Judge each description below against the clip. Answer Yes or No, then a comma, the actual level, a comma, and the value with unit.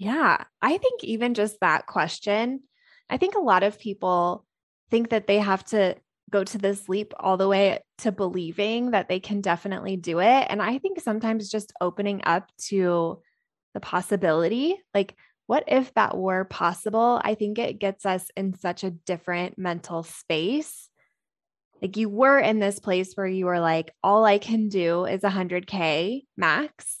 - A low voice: No, high, 200 Hz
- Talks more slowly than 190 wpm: Yes, average, 170 wpm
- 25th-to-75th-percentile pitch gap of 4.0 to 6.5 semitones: No, average, 3.4 semitones